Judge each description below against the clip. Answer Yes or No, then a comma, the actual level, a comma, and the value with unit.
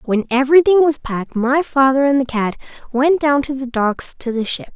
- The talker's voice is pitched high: Yes, very high, 265 Hz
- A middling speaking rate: No, fast, 215 wpm